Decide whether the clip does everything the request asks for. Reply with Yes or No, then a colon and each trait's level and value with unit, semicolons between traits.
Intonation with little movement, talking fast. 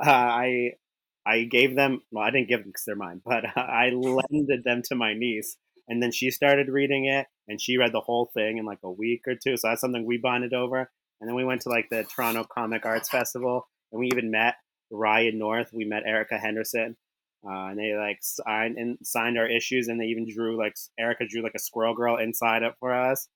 Yes: narrow, 2.0 semitones; fast, 230 wpm